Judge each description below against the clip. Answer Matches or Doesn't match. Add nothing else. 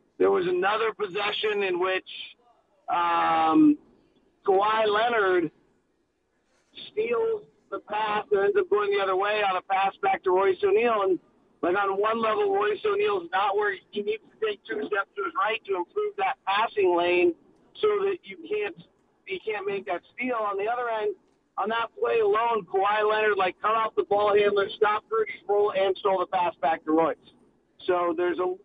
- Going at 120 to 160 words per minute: Doesn't match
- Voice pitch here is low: Doesn't match